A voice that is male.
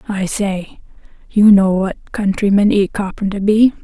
No: female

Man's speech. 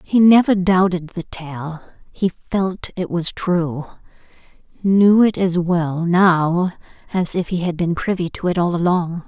No: female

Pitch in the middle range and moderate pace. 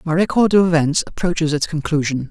Yes: medium, 160 Hz; average, 180 wpm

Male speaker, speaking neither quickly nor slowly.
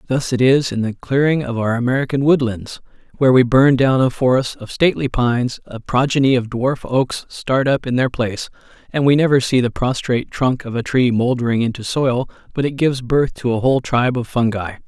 No: male; fast, 210 wpm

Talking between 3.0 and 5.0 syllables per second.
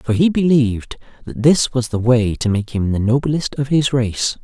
Yes: 4.6 syllables/s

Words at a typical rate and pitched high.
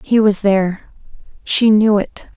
Yes: average, 155 wpm; high, 205 Hz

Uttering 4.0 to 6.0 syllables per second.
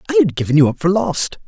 No: 6.7 syllables/s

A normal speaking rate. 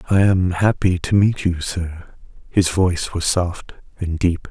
Yes: average, 175 wpm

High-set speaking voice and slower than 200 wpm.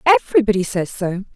Yes: high, 215 Hz; slow, 135 wpm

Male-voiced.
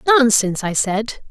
No: female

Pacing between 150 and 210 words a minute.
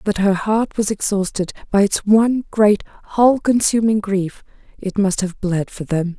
Yes: average, 185 wpm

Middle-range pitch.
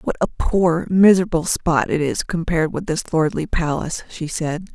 Yes: medium, 165 Hz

